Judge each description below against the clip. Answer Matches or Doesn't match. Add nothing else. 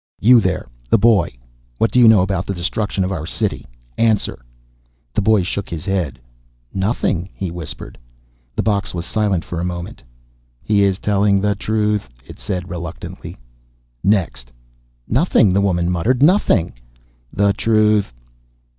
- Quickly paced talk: Doesn't match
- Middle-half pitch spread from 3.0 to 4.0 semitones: Matches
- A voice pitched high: Doesn't match